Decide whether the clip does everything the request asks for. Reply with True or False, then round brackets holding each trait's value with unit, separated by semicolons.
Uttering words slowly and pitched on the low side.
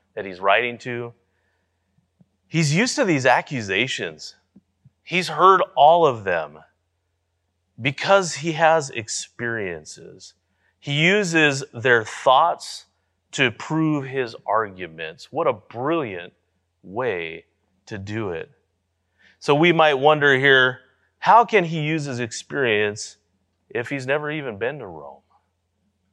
True (115 wpm; 125 Hz)